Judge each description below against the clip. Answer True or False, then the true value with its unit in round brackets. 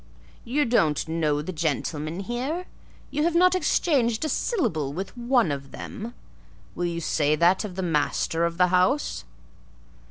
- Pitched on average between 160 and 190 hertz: True (185 Hz)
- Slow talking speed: False (155 wpm)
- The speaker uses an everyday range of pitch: False (7.7 semitones)